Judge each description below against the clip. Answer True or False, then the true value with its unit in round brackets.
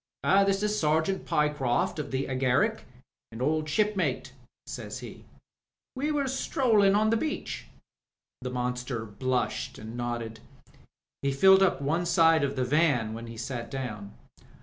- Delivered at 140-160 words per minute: True (145 wpm)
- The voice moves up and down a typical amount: False (7.8 semitones)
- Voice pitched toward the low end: False (145 Hz)